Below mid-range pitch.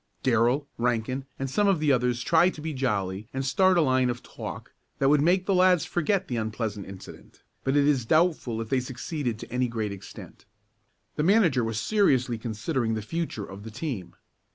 Yes: low, 130 Hz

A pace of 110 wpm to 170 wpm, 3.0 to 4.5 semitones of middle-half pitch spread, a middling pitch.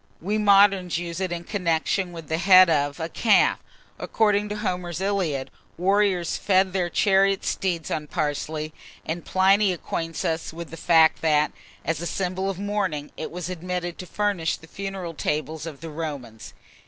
Yes: average, 165 wpm; average, 3.3 semitones; medium, 175 Hz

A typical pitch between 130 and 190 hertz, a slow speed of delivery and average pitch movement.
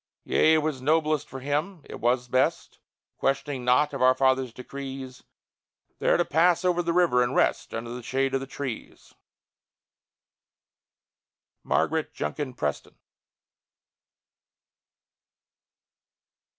Yes: low, 135 Hz; slow, 115 wpm; average, 3.2 semitones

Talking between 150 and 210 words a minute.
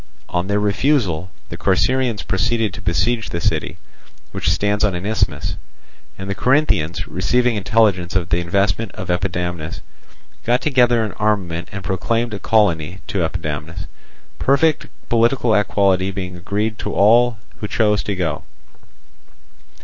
No: average, 140 wpm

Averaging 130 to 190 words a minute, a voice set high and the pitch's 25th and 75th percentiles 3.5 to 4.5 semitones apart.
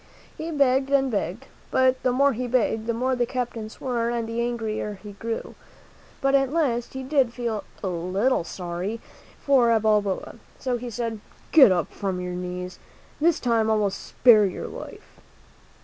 Yes: average, 170 wpm; high, 235 Hz; average, 3.8 semitones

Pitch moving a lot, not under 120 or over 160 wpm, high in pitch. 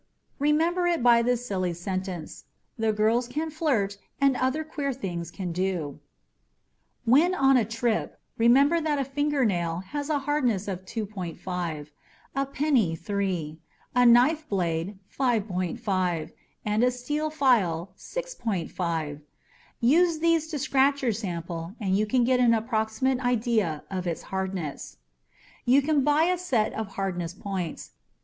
Yes: wide, 6.9 semitones; average, 140 wpm; high, 225 Hz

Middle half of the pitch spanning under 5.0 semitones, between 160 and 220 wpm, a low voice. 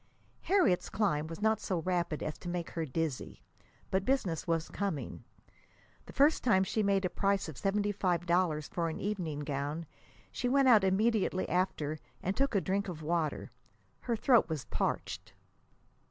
No: average, 4.1 semitones; average, 170 wpm; medium, 185 Hz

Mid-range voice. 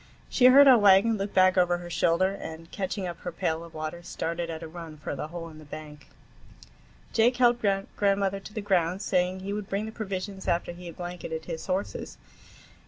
Yes: medium, 180 Hz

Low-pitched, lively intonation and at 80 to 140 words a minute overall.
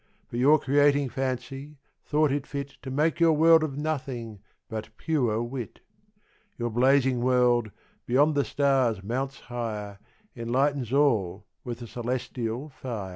No: low, 130 Hz; average, 3.3 semitones; slow, 135 wpm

